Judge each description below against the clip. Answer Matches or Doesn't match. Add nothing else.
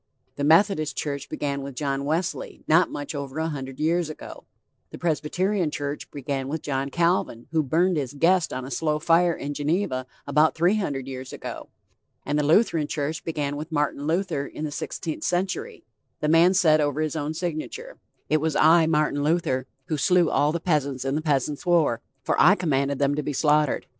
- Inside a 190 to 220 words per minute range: Matches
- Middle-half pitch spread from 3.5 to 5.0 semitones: Doesn't match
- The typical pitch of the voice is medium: Matches